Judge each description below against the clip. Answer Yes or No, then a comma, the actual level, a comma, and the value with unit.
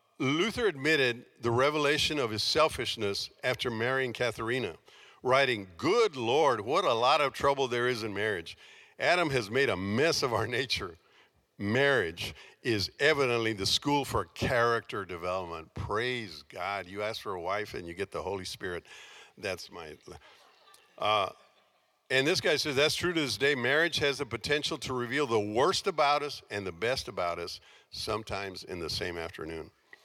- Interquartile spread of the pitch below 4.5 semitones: No, average, 5.2 semitones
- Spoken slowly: No, average, 165 wpm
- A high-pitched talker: No, low, 125 Hz